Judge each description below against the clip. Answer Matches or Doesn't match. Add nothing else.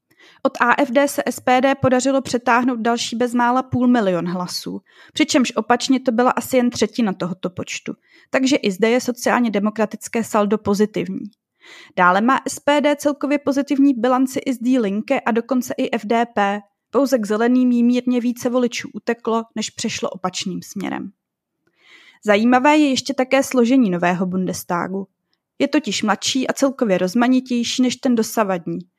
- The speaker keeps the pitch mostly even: Doesn't match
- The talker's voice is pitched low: Doesn't match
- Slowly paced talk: Doesn't match